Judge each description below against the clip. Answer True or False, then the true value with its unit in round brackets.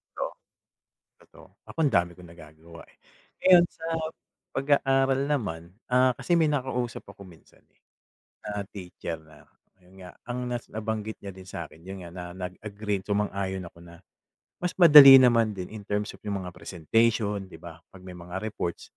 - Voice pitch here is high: False (100 Hz)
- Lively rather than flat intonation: True (5.8 semitones)